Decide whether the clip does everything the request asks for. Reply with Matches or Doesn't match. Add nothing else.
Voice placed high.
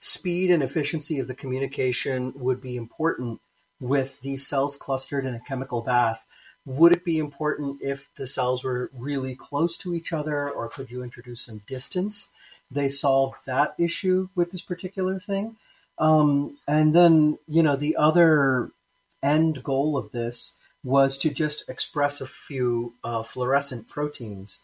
Doesn't match